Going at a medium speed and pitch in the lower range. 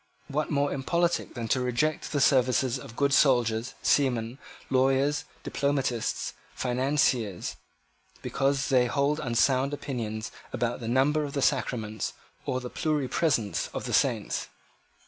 No: slow, 125 wpm; low, 130 Hz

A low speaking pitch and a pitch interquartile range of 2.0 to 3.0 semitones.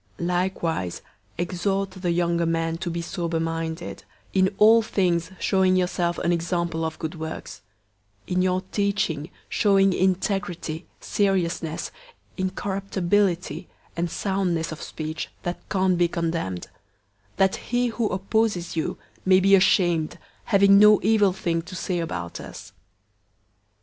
No: medium, 180 Hz; narrow, 2.6 semitones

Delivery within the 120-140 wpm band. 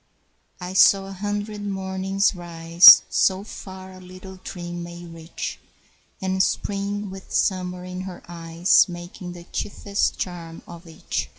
Yes: slow, 135 wpm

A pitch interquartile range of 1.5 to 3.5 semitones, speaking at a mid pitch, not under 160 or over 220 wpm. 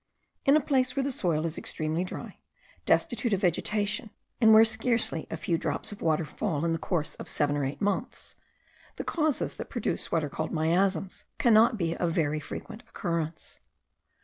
No: wide, 5.6 semitones; medium, 180 Hz; average, 180 wpm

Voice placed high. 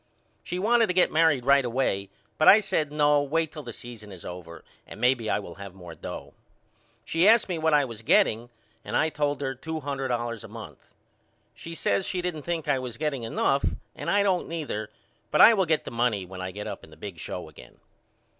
No: low, 135 Hz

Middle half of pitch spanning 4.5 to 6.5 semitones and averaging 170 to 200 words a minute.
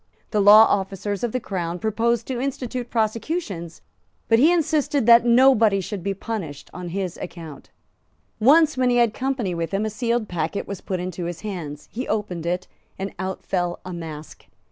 Yes: average, 5.1 semitones; average, 180 wpm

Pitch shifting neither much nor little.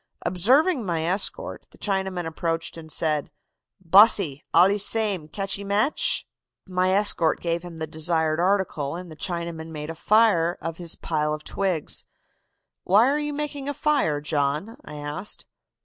Yes: average, 4.2 semitones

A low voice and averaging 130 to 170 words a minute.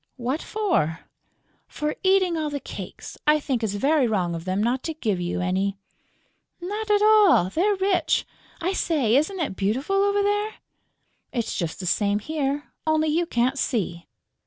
No: very high, 290 Hz; average, 165 wpm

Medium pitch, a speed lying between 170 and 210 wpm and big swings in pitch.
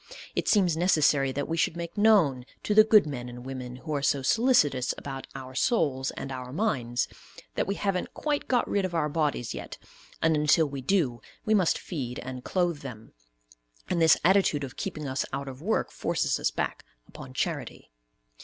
Yes: medium, 150 Hz; average, 190 wpm; wide, 5.9 semitones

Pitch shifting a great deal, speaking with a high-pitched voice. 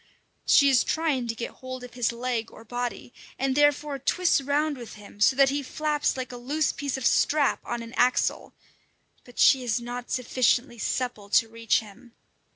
No: average, 2.8 semitones; very high, 250 Hz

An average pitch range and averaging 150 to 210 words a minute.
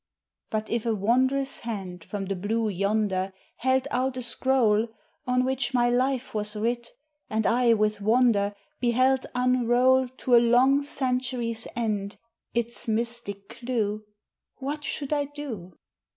No: average, 3.3 semitones; slow, 135 wpm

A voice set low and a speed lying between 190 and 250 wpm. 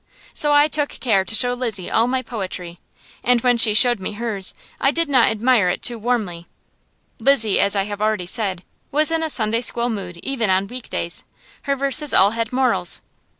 No: high, 230 Hz; average, 195 wpm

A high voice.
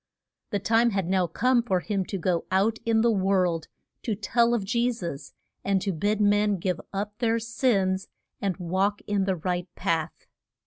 Yes: high, 200 Hz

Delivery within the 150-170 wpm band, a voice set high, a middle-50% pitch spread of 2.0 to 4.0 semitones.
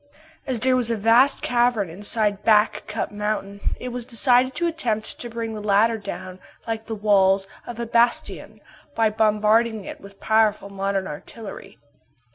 Yes: average, 160 wpm; high, 220 Hz; narrow, 2.6 semitones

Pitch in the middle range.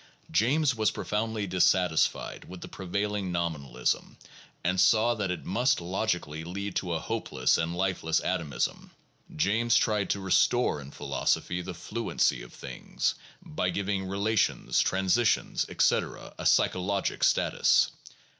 No: very low, 95 Hz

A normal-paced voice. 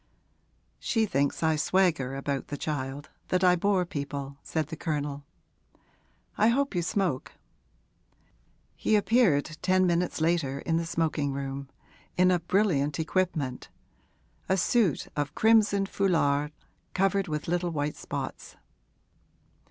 No: slow, 125 wpm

